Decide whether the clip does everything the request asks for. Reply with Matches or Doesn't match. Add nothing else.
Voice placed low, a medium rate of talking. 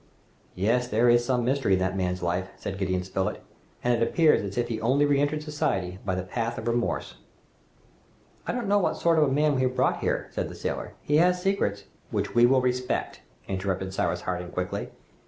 Doesn't match